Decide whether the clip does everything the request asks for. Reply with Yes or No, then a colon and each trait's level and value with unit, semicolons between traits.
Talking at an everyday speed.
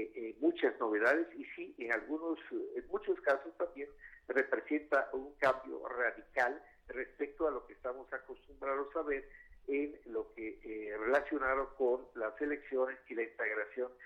Yes: average, 140 wpm